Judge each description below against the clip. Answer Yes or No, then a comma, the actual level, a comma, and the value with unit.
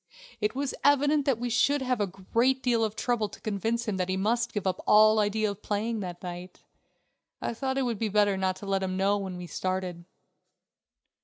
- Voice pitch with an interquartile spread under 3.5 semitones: No, average, 3.8 semitones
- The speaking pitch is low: No, high, 210 Hz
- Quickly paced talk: Yes, fast, 215 wpm